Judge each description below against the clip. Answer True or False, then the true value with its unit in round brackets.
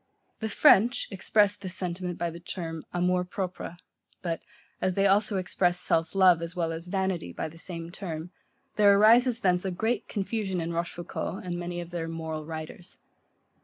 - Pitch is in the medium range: True (180 Hz)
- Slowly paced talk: False (170 wpm)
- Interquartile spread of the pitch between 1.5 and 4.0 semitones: True (2.6 semitones)